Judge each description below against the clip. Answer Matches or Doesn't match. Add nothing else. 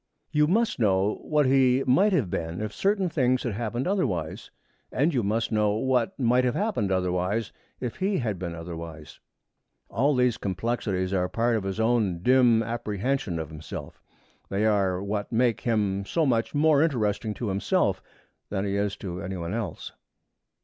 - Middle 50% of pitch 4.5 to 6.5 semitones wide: Matches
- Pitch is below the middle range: Matches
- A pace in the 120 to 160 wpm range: Doesn't match